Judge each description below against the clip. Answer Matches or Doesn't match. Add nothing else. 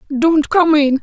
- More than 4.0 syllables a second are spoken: Doesn't match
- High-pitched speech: Matches